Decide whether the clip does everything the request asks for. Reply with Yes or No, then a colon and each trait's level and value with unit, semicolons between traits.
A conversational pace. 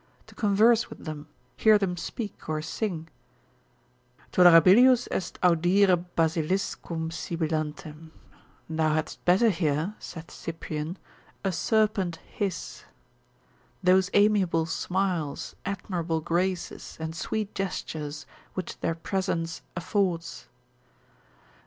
No: slow, 95 wpm